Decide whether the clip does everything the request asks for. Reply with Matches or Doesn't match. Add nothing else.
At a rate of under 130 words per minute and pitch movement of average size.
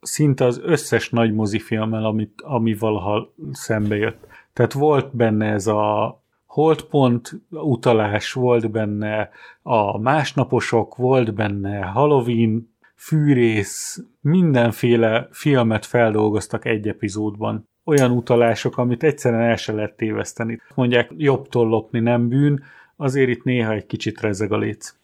Matches